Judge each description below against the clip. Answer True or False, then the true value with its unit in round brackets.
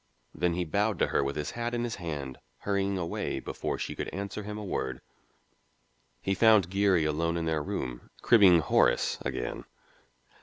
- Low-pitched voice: True (90 Hz)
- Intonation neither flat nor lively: True (4.7 semitones)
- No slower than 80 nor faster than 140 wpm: False (175 wpm)